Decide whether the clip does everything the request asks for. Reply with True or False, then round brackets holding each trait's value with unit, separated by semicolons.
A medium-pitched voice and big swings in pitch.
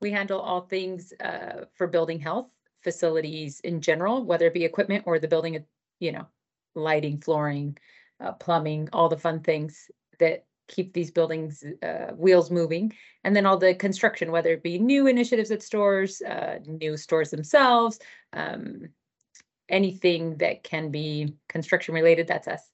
False (170 Hz; 3.8 semitones)